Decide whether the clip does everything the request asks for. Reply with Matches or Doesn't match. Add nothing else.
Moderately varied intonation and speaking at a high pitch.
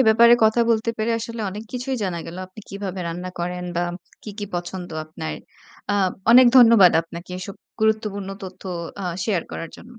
Matches